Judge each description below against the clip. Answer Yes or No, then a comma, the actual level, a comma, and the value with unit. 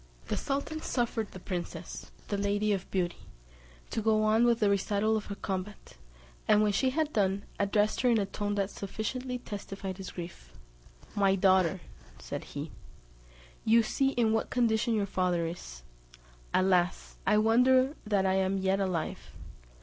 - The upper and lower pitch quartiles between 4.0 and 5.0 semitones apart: No, average, 2.8 semitones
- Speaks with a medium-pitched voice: No, high, 205 Hz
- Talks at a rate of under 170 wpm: Yes, average, 160 wpm